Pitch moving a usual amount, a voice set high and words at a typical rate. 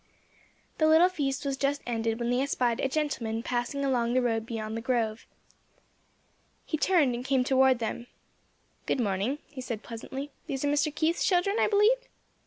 Yes: average, 3.9 semitones; very high, 265 Hz; average, 175 wpm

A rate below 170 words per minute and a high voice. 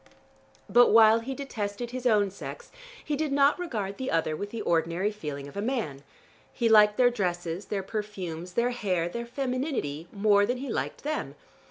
No: average, 180 wpm; high, 210 Hz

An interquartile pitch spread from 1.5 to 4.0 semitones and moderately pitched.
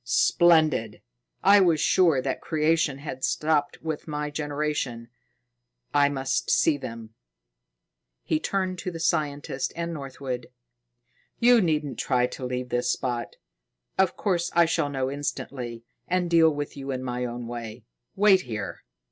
No: average, 4.5 semitones; medium, 145 Hz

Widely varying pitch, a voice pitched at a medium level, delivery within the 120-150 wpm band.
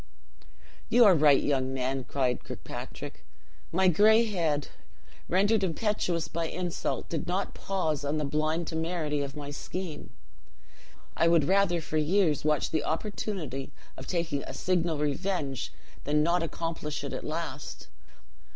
No: average, 3.8 semitones; medium, 160 Hz; average, 140 wpm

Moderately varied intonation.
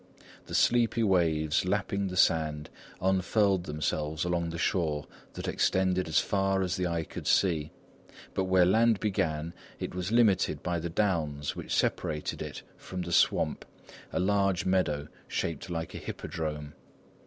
Yes: average, 3.4 semitones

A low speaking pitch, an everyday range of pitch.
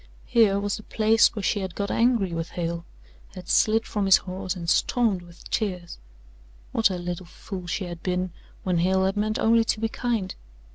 No: high, 190 Hz; average, 3.3 semitones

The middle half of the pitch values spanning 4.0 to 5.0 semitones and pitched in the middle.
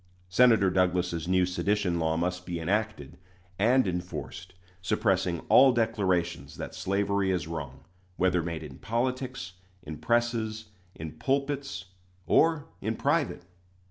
No: average, 4.3 semitones; very low, 95 Hz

